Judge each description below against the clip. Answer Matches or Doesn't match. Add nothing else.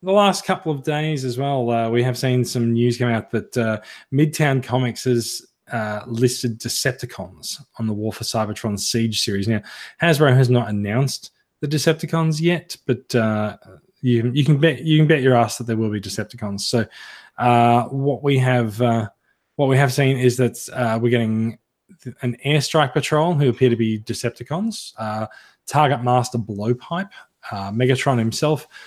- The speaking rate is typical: Matches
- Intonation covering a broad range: Doesn't match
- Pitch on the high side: Doesn't match